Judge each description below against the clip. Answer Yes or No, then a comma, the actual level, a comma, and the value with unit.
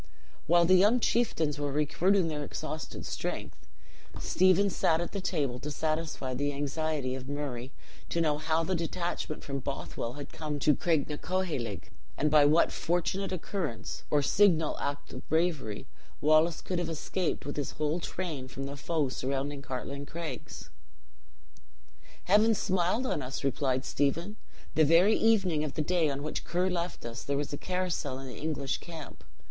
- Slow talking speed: No, average, 165 wpm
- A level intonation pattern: No, average, 3.7 semitones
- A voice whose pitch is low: No, medium, 155 Hz